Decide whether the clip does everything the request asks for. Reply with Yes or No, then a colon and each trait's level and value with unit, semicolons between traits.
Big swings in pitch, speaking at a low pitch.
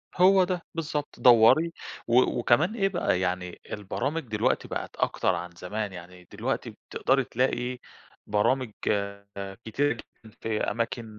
Yes: wide, 5.9 semitones; low, 120 Hz